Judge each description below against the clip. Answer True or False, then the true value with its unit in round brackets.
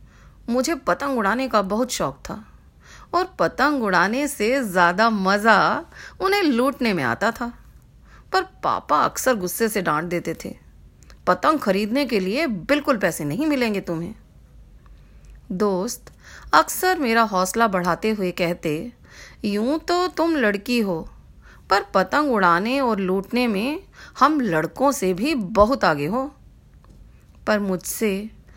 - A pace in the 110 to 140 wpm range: True (130 wpm)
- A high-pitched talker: True (225 Hz)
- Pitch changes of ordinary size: False (6.4 semitones)